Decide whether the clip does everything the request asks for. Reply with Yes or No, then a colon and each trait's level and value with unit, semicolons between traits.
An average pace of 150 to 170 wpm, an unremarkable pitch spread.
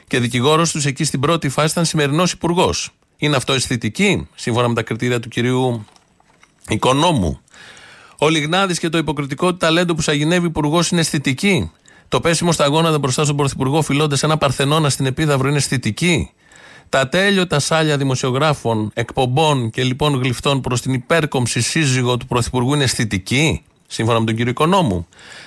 Yes: average, 160 wpm; average, 3.9 semitones